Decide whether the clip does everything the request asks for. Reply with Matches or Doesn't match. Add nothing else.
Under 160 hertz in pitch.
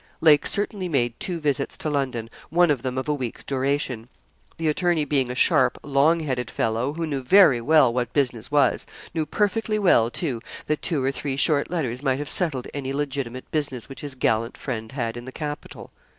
Matches